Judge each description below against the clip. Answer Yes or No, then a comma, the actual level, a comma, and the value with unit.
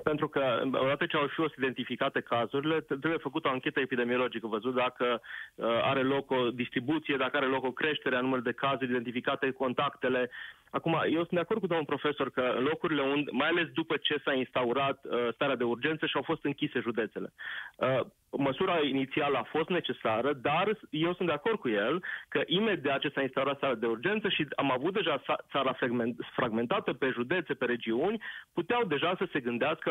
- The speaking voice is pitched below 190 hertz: Yes, medium, 140 Hz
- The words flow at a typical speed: No, fast, 180 wpm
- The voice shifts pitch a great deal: No, average, 3.8 semitones